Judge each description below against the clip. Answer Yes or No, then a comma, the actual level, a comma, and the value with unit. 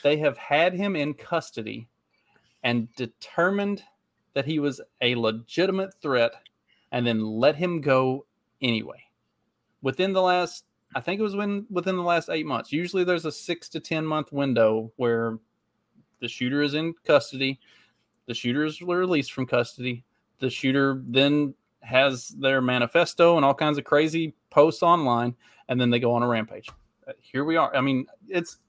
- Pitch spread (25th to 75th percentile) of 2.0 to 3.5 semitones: No, wide, 5.6 semitones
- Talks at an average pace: Yes, average, 165 wpm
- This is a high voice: No, medium, 140 Hz